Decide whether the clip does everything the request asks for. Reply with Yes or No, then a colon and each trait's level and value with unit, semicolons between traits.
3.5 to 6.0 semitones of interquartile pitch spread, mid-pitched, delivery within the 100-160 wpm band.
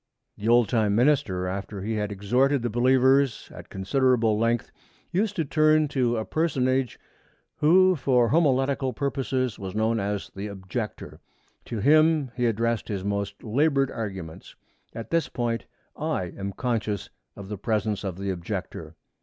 No: average, 4.8 semitones; low, 115 Hz; average, 150 wpm